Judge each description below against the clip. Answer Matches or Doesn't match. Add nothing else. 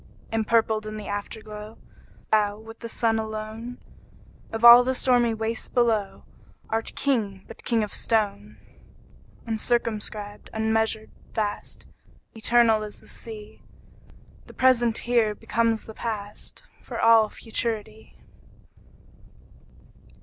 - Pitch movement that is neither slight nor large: Doesn't match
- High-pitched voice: Matches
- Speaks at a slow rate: Matches